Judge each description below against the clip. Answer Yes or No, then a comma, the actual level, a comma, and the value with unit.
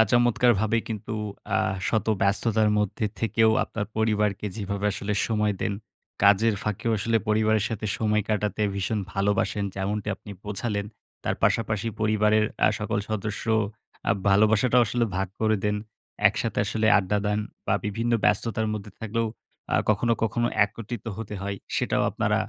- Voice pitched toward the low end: Yes, low, 105 Hz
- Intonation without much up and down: Yes, narrow, 1.6 semitones